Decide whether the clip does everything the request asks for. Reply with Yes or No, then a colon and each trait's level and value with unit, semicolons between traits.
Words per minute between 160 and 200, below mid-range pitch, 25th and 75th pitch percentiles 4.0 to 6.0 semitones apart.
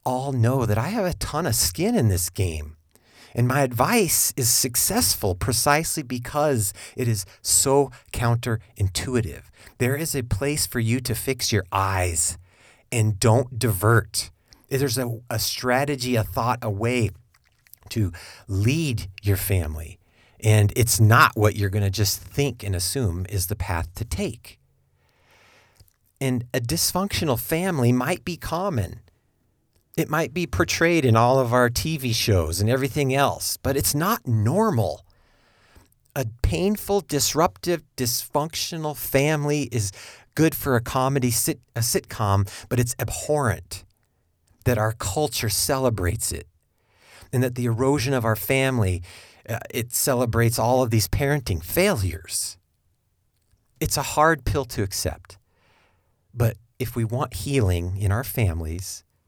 No: average, 140 wpm; low, 115 Hz; average, 5.0 semitones